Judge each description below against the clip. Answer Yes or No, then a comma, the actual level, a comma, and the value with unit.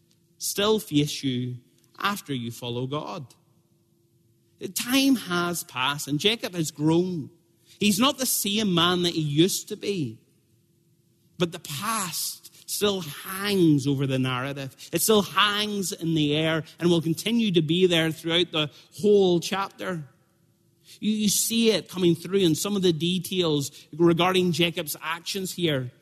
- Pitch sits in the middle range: Yes, medium, 170 Hz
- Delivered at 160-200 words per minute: No, average, 145 wpm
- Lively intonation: No, average, 4.1 semitones